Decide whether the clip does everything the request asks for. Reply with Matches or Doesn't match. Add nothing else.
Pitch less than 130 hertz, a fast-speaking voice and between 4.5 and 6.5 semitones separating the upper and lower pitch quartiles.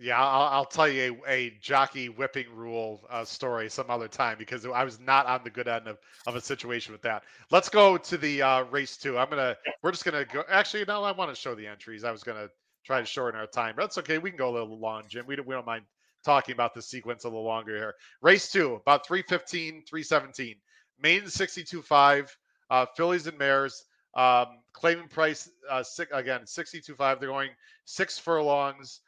Doesn't match